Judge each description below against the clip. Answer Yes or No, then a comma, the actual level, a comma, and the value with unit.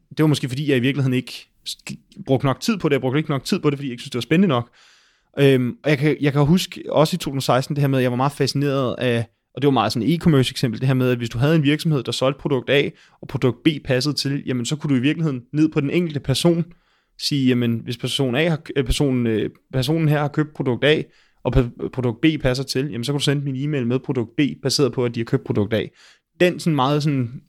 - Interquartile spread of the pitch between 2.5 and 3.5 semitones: Yes, average, 2.9 semitones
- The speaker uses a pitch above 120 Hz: Yes, medium, 140 Hz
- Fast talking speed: Yes, fast, 275 wpm